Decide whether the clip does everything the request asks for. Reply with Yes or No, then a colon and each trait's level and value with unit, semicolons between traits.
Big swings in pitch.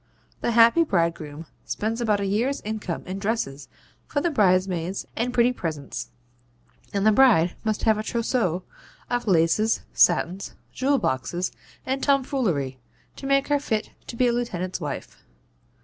Yes: wide, 5.7 semitones